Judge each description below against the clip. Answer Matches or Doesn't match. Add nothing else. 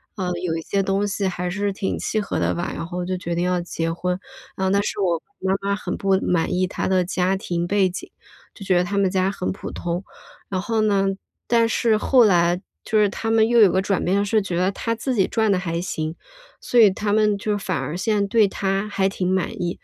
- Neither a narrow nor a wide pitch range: Doesn't match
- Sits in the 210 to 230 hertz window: Doesn't match